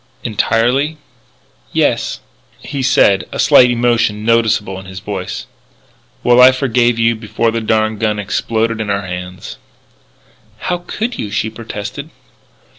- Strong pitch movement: No, average, 2.8 semitones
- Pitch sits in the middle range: No, low, 110 Hz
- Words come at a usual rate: No, slow, 130 wpm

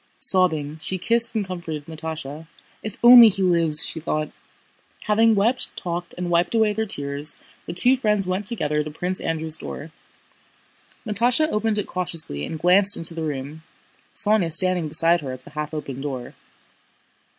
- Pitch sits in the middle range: Yes, medium, 170 Hz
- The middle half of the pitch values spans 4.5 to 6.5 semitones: Yes, average, 5.2 semitones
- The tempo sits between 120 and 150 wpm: No, average, 160 wpm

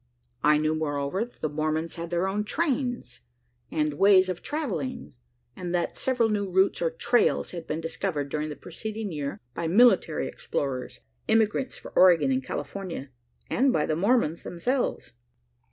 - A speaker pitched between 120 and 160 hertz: No, medium, 170 Hz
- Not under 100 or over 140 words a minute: No, average, 155 wpm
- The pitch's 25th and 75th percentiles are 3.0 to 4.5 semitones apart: No, wide, 5.5 semitones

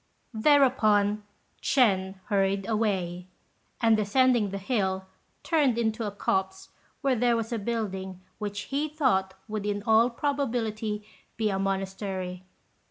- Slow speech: Yes, slow, 125 wpm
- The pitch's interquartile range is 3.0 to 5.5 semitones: Yes, average, 3.5 semitones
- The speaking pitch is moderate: No, high, 210 Hz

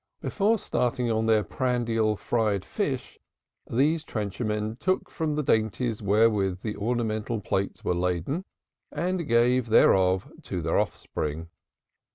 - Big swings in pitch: No, average, 3.8 semitones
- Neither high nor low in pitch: No, low, 110 Hz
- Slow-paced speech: Yes, slow, 130 wpm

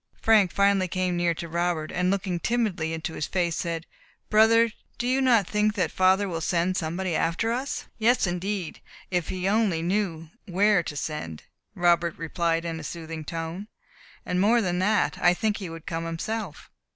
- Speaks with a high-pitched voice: No, medium, 180 Hz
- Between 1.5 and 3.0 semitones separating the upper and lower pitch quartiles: No, average, 3.8 semitones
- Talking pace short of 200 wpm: Yes, average, 175 wpm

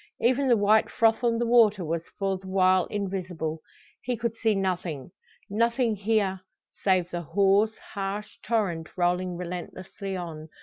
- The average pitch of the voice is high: Yes, high, 195 Hz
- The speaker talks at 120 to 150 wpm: Yes, average, 145 wpm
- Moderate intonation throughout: Yes, average, 3.6 semitones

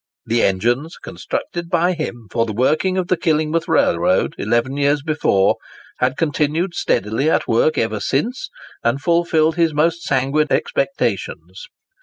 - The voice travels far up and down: Yes, wide, 6.0 semitones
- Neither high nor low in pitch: Yes, medium, 150 Hz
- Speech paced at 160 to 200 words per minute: No, average, 140 wpm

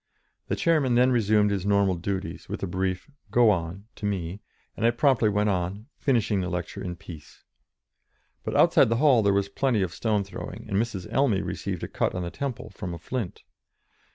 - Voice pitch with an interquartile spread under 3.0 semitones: No, average, 3.9 semitones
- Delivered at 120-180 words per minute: No, average, 195 wpm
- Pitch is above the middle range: No, low, 100 Hz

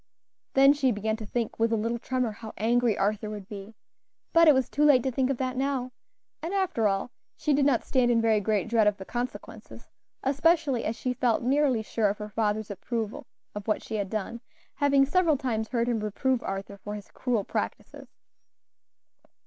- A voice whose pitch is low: No, high, 235 Hz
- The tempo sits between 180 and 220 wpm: Yes, average, 195 wpm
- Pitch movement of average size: Yes, average, 3.8 semitones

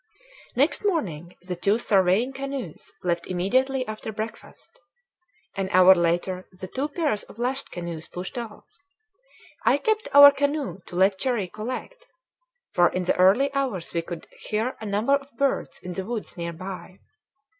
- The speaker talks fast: No, average, 155 wpm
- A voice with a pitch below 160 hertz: No, high, 210 Hz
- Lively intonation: Yes, wide, 6.8 semitones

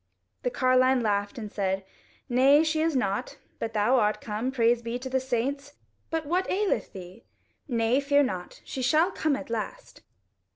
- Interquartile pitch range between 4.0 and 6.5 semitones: Yes, average, 4.3 semitones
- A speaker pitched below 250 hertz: No, very high, 255 Hz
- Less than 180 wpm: Yes, average, 170 wpm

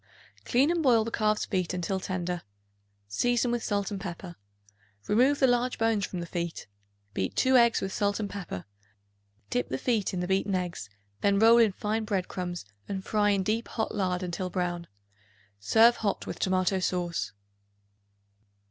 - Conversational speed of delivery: Yes, average, 170 wpm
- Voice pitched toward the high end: Yes, high, 195 Hz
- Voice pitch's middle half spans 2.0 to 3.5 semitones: No, average, 3.9 semitones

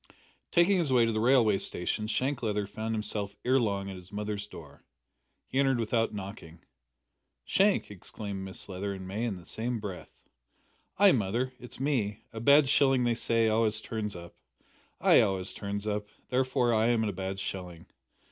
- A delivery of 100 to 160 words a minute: No, average, 175 wpm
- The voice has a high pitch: No, low, 110 Hz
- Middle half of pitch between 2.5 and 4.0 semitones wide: Yes, average, 3.7 semitones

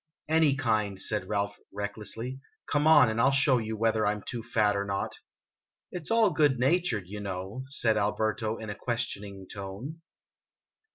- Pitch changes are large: No, average, 4.6 semitones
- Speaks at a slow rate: No, average, 185 wpm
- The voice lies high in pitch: No, low, 110 Hz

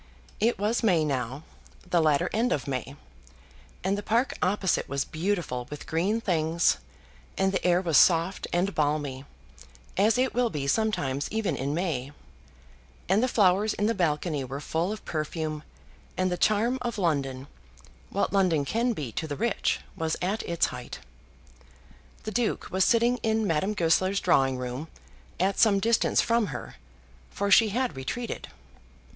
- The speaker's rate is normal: Yes, average, 160 wpm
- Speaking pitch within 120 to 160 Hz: No, medium, 180 Hz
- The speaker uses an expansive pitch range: Yes, wide, 6.3 semitones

